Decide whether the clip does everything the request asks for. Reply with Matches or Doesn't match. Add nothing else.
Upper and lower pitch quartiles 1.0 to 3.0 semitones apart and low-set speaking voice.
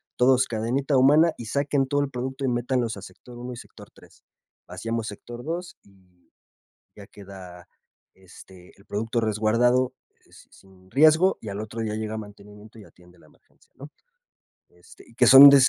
Doesn't match